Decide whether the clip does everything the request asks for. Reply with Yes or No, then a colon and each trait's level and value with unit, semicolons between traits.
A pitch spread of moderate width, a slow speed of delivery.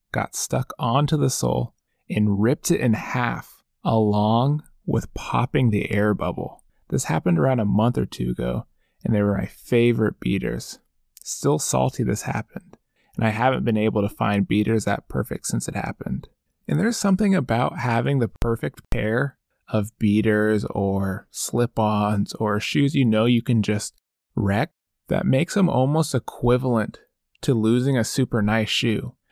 No: average, 3.6 semitones; average, 160 wpm